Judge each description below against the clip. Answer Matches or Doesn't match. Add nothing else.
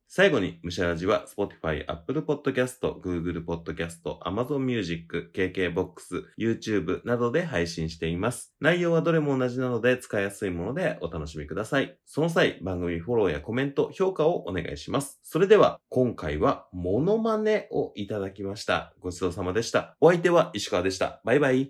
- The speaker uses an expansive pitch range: Matches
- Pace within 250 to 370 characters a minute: Doesn't match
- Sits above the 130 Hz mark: Doesn't match